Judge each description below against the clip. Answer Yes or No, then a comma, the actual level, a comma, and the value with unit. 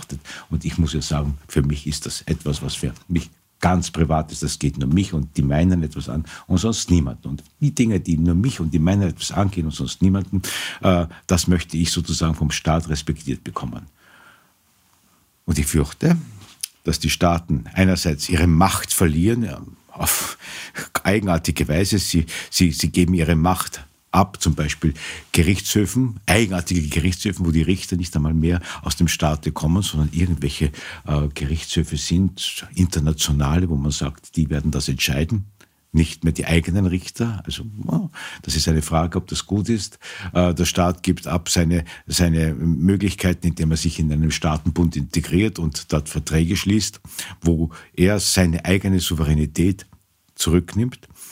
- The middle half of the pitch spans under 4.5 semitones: Yes, average, 2.7 semitones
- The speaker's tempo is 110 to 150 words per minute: No, average, 160 wpm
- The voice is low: Yes, very low, 85 Hz